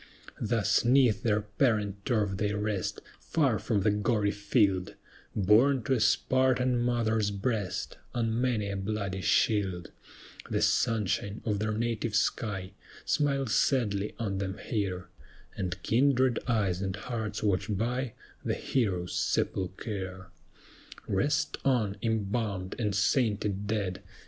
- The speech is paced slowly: Yes, slow, 125 wpm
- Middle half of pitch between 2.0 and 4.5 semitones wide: Yes, average, 3.2 semitones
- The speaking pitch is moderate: No, low, 105 Hz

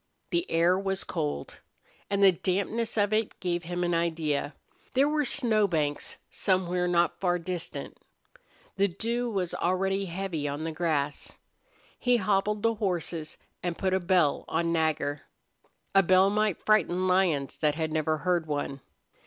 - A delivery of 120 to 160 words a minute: Yes, average, 155 wpm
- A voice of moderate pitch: Yes, medium, 180 Hz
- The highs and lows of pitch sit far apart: No, average, 3.5 semitones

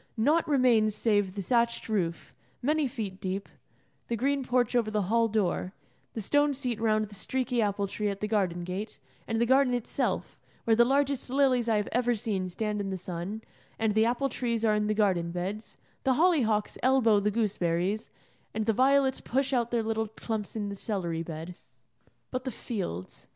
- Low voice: No, high, 220 Hz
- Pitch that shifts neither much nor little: Yes, average, 3.6 semitones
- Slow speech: No, average, 190 wpm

